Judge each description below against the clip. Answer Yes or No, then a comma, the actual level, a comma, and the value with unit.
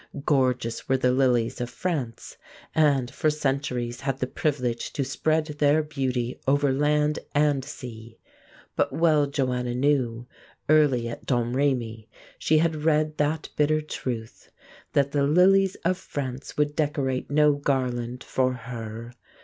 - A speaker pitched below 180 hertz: Yes, low, 135 Hz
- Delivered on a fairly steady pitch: No, average, 3.2 semitones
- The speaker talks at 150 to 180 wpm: No, slow, 135 wpm